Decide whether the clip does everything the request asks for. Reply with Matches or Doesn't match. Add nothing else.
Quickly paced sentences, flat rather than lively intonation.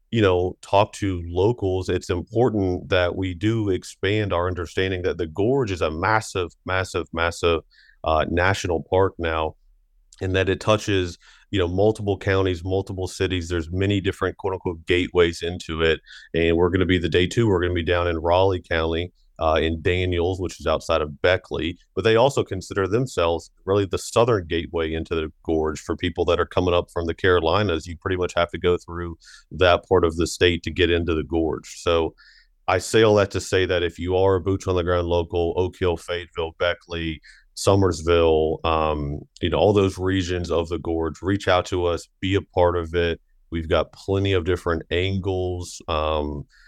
Doesn't match